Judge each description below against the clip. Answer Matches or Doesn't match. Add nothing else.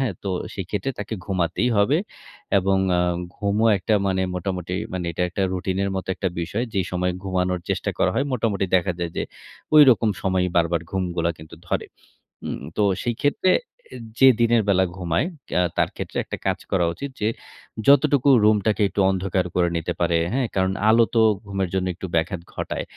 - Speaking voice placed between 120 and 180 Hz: Doesn't match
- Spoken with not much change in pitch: Doesn't match